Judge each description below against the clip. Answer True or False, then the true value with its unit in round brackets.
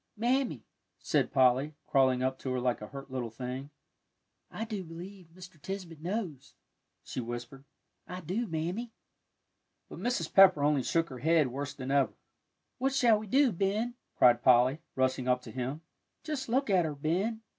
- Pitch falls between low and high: True (155 Hz)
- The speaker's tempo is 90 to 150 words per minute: False (165 wpm)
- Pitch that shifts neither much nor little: False (7.4 semitones)